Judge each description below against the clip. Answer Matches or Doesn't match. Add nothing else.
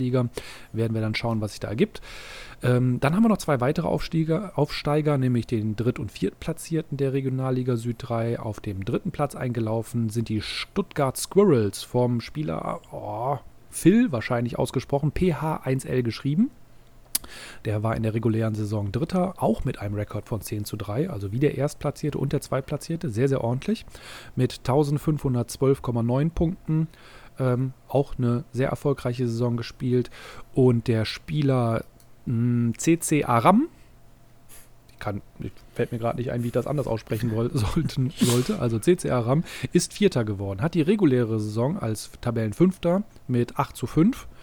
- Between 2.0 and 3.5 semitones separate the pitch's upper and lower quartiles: Doesn't match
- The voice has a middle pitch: Doesn't match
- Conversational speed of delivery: Matches